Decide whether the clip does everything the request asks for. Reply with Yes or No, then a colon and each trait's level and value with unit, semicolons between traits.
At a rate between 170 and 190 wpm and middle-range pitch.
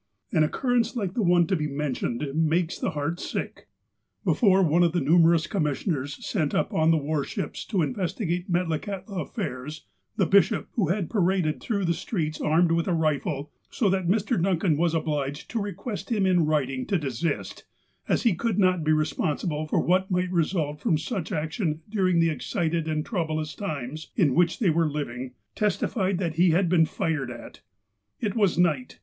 Yes: average, 180 wpm; medium, 170 Hz